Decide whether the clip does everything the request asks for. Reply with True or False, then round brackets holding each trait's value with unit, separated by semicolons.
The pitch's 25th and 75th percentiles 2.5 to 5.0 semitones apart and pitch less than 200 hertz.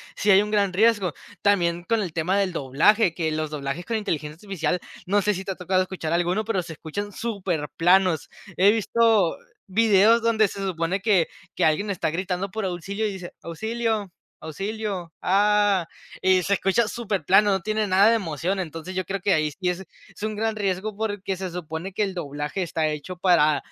True (3.5 semitones; 190 Hz)